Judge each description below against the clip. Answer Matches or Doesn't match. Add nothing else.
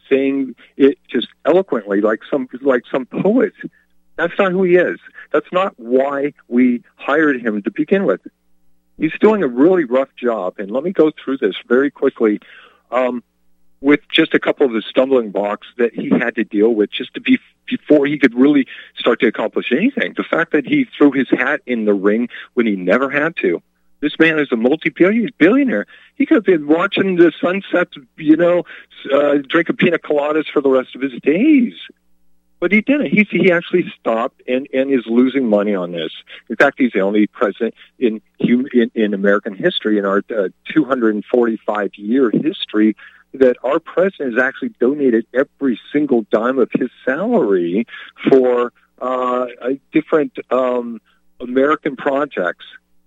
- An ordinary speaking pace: Matches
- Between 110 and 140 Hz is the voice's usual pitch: Matches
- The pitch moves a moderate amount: Doesn't match